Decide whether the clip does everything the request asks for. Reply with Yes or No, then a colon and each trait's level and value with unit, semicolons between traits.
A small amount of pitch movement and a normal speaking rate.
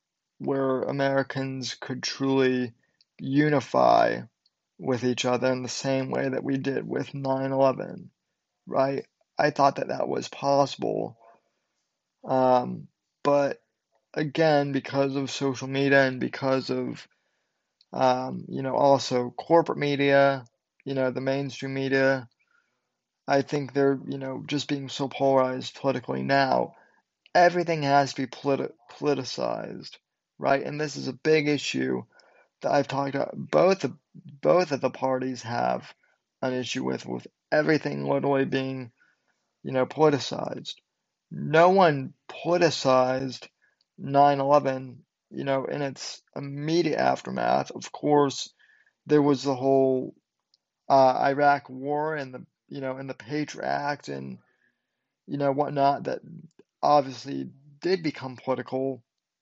No: narrow, 1.7 semitones; slow, 125 wpm